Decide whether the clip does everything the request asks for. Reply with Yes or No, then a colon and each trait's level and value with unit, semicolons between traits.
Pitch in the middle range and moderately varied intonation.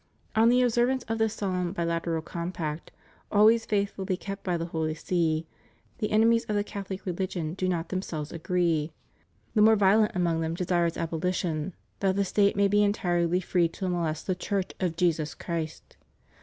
Yes: medium, 180 Hz; average, 3.4 semitones